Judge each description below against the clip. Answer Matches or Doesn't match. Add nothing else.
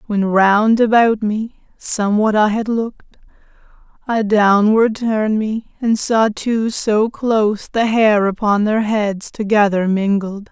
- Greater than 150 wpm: Doesn't match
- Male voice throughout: Doesn't match